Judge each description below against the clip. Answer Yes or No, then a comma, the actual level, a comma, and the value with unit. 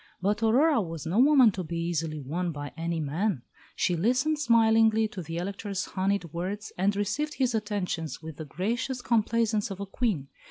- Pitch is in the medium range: No, high, 200 Hz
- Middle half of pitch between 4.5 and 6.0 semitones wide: Yes, average, 5.1 semitones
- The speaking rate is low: No, average, 175 wpm